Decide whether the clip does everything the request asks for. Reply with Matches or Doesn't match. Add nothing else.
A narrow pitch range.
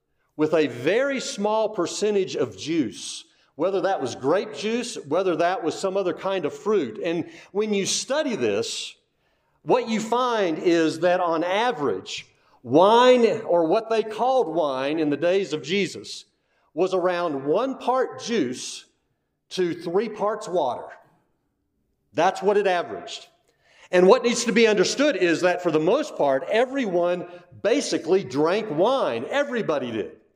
Doesn't match